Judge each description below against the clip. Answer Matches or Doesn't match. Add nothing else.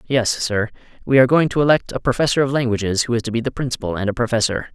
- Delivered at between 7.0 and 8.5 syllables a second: Matches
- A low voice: Matches